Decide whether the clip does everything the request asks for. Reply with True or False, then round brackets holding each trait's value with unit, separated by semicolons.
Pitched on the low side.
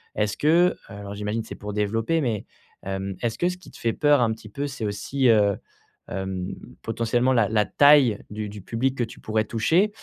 True (115 Hz)